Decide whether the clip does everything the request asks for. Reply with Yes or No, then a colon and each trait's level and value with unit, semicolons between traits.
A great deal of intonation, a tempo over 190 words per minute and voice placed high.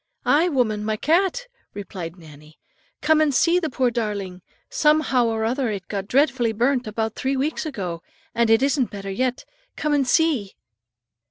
No: wide, 5.8 semitones; average, 165 wpm; high, 240 Hz